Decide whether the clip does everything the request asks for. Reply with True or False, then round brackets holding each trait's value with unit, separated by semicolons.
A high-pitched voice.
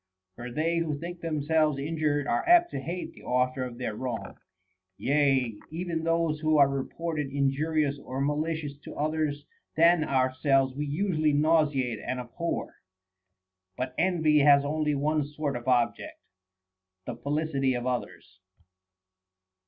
False (145 Hz)